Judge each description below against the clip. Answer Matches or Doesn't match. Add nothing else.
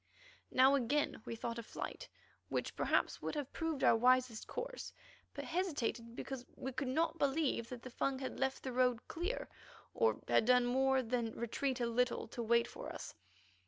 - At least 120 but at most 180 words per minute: Matches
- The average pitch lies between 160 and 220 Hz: Doesn't match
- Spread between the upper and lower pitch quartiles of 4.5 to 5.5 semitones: Doesn't match